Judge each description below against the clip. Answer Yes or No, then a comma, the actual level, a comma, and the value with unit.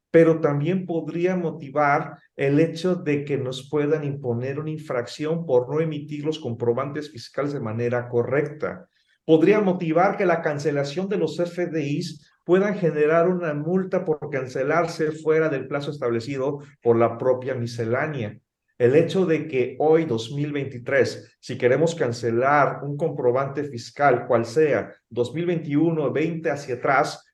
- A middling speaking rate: Yes, average, 135 wpm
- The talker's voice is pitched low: No, medium, 150 Hz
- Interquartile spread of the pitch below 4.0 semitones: Yes, average, 3.6 semitones